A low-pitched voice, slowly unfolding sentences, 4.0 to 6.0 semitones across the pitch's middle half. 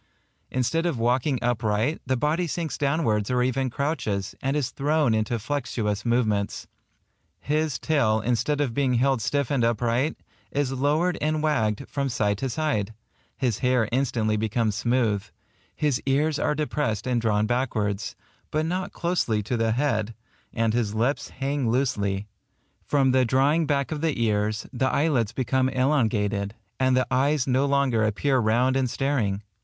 No: low, 125 Hz; average, 155 wpm; average, 4.4 semitones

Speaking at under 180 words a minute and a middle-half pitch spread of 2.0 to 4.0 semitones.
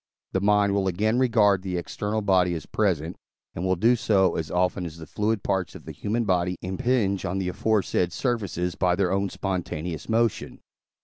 No: average, 185 wpm; average, 2.7 semitones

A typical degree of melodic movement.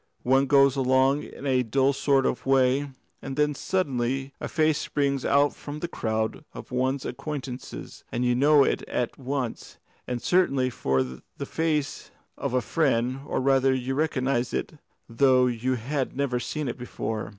No: narrow, 2.1 semitones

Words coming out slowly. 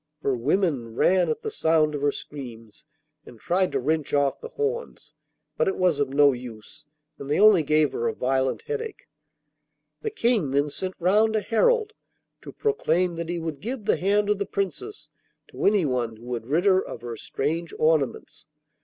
No: average, 185 wpm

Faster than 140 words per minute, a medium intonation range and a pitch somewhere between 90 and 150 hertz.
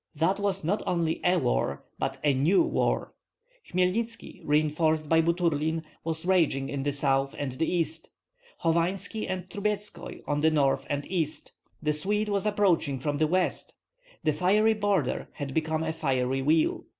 No: average, 160 wpm; average, 4.2 semitones; medium, 160 Hz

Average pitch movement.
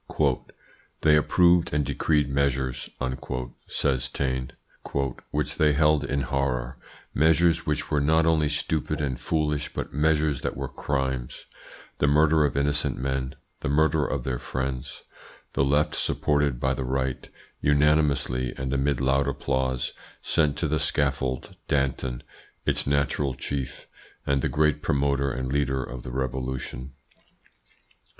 No: narrow, 2.3 semitones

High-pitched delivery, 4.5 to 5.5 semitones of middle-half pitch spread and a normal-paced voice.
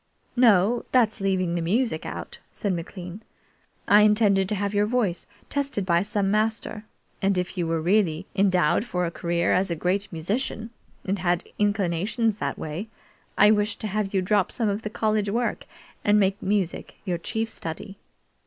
No: high, 200 Hz; average, 3.1 semitones; average, 170 wpm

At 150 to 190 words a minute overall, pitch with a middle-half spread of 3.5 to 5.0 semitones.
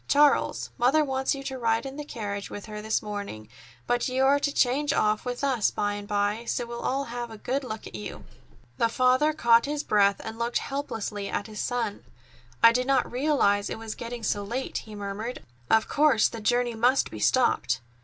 No: fast, 205 wpm; average, 3.9 semitones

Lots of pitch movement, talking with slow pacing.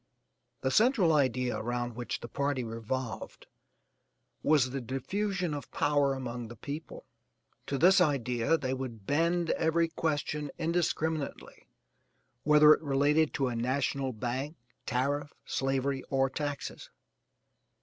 No: average, 3.5 semitones; slow, 120 wpm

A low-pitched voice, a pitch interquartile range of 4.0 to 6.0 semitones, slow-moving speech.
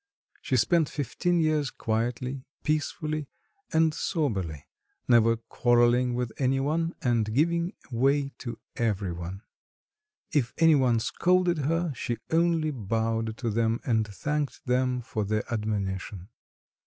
Yes: low, 125 Hz; wide, 5.4 semitones; slow, 125 wpm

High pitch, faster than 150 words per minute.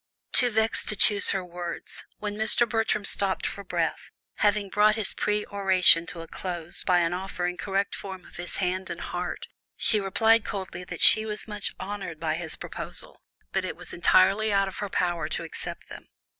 Yes: high, 195 Hz; average, 190 wpm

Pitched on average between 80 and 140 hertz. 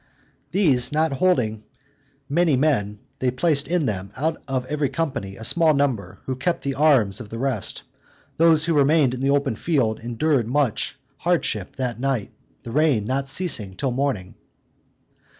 Yes: low, 135 Hz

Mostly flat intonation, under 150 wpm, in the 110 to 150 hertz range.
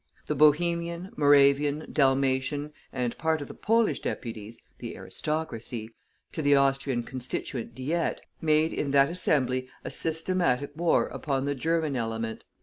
No: average, 3.7 semitones; slow, 135 wpm; medium, 140 Hz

